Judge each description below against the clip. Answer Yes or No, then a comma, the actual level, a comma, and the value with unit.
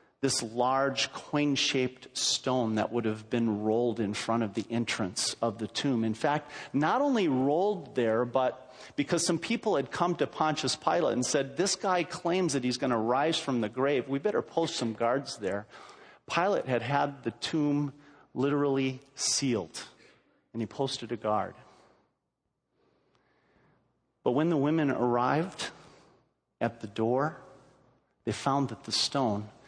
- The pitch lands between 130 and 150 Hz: Yes, low, 135 Hz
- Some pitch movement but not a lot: Yes, average, 3.8 semitones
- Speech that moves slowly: No, average, 155 wpm